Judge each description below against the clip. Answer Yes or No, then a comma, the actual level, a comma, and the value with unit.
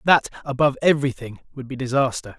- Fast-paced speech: No, average, 150 wpm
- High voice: No, low, 135 Hz